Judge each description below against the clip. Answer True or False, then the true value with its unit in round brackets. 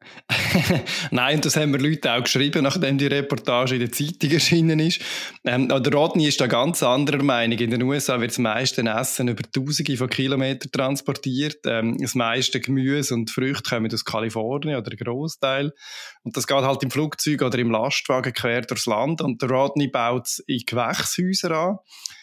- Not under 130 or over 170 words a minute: False (185 wpm)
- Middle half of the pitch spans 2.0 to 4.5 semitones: True (2.9 semitones)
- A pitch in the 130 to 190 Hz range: True (135 Hz)